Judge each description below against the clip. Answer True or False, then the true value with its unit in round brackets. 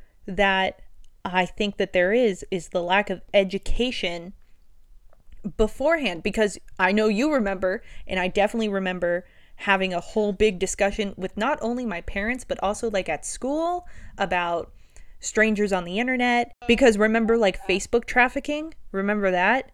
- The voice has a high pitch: True (205 Hz)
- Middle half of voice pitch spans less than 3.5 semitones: False (3.9 semitones)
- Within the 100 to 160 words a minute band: True (145 wpm)